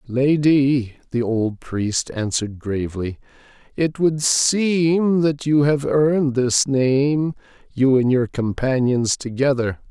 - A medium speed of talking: No, slow, 120 wpm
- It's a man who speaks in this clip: Yes, male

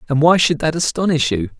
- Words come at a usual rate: No, fast, 225 wpm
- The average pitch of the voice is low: No, medium, 155 Hz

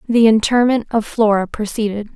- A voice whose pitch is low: No, high, 220 Hz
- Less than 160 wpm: Yes, average, 140 wpm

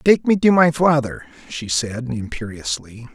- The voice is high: No, low, 130 Hz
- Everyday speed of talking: Yes, average, 155 wpm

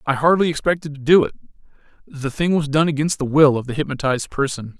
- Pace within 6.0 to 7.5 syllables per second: Yes, 6.4 syllables/s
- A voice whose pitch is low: No, medium, 145 Hz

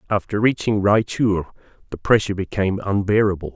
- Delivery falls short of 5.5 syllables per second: No, 5.9 syllables/s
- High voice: No, low, 100 Hz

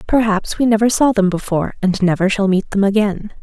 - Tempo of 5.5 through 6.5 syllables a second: Yes, 5.8 syllables/s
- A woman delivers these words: Yes, female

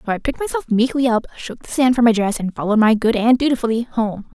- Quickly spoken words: Yes, fast, 260 wpm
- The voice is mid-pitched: No, high, 230 Hz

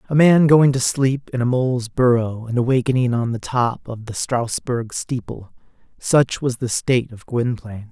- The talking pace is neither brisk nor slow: Yes, average, 180 wpm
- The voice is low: Yes, low, 125 Hz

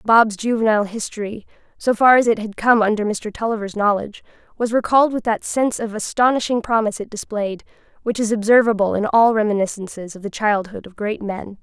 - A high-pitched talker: Yes, high, 215 Hz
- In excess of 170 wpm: Yes, average, 180 wpm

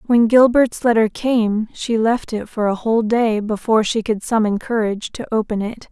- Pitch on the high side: Yes, high, 220 Hz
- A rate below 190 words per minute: No, average, 195 wpm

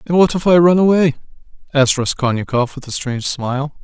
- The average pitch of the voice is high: No, medium, 145 Hz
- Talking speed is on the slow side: No, average, 190 wpm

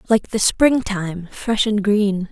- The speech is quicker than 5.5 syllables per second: No, 3.4 syllables/s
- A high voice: Yes, high, 205 Hz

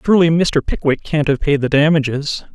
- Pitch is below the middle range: No, medium, 150 Hz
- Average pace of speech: Yes, average, 190 wpm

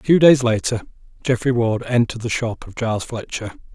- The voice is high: No, low, 115 Hz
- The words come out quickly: No, average, 190 wpm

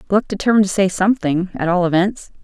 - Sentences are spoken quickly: No, average, 195 wpm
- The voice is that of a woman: Yes, female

